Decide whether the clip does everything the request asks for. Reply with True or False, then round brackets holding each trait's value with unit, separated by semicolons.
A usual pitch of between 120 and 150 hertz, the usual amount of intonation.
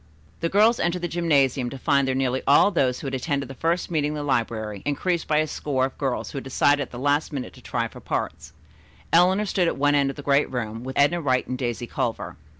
True (140 Hz; 3.5 semitones)